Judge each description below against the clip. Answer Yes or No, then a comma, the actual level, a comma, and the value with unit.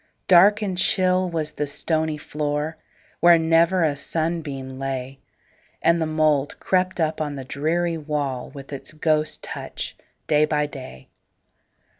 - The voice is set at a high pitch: No, medium, 155 Hz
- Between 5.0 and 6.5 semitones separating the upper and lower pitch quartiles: No, narrow, 2.5 semitones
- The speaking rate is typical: No, slow, 125 wpm